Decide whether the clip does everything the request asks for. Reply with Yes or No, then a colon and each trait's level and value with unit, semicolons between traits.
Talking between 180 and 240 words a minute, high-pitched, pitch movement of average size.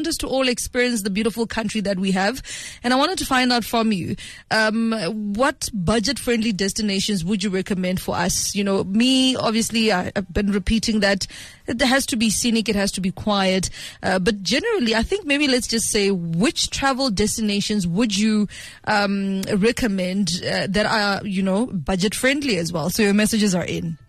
Yes: average, 190 wpm; high, 215 Hz; average, 3.1 semitones